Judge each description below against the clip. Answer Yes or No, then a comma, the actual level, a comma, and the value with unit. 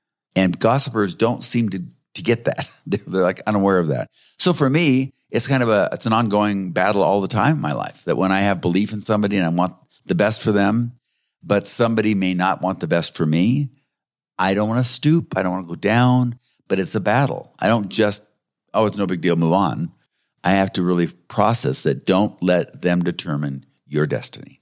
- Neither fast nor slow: No, fast, 220 wpm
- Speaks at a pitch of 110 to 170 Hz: No, low, 100 Hz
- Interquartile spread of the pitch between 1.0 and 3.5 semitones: No, average, 4.2 semitones